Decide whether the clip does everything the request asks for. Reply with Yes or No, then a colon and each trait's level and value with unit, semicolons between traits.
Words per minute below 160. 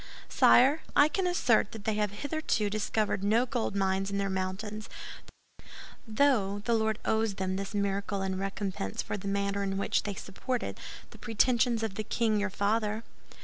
No: average, 170 wpm